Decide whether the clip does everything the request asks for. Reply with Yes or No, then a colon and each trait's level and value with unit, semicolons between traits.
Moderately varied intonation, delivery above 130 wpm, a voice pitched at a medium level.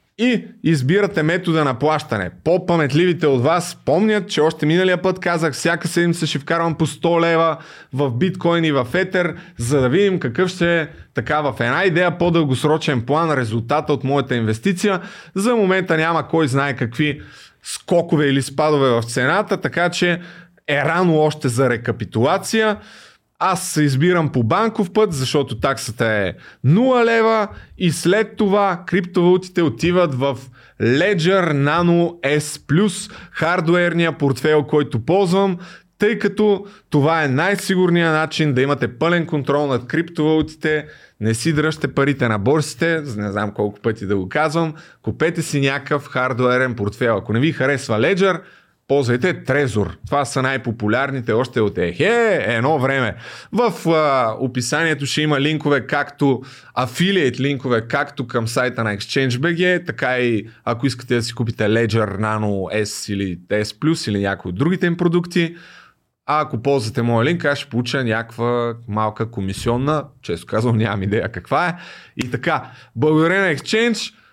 No: wide, 5.7 semitones; average, 150 wpm; medium, 150 Hz